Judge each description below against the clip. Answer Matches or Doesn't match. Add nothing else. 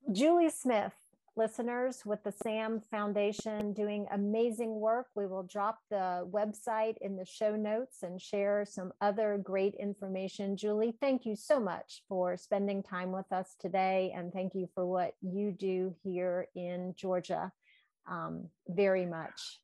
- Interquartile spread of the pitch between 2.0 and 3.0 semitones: Matches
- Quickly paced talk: Doesn't match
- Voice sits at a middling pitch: Doesn't match